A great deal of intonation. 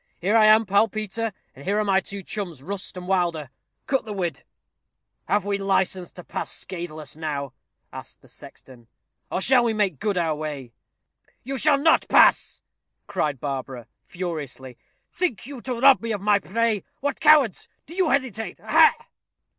Yes: wide, 6.2 semitones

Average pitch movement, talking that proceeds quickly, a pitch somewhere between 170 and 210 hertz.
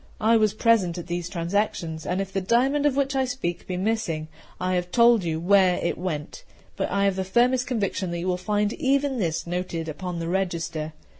Yes: average, 4.9 semitones; fast, 210 wpm; medium, 185 Hz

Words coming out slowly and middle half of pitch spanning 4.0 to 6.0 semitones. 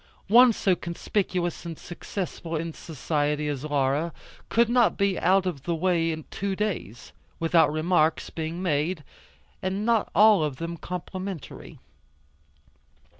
No: slow, 125 wpm; average, 3.5 semitones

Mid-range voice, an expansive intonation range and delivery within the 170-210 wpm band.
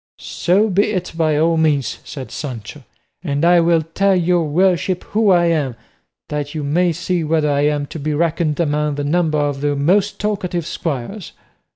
No: medium, 160 Hz; average, 3.3 semitones; average, 180 wpm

